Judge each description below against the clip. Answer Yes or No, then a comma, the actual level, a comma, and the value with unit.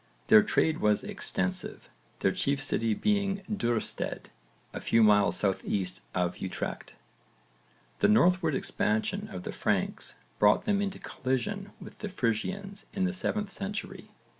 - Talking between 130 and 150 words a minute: Yes, average, 140 wpm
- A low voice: No, medium, 145 Hz